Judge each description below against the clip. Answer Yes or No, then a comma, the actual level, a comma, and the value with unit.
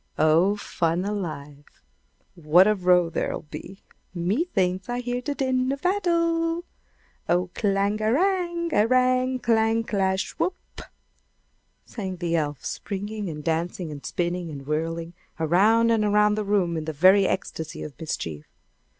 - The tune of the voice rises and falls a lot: Yes, wide, 5.9 semitones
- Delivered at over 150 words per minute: No, average, 145 wpm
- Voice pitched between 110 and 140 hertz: No, high, 195 Hz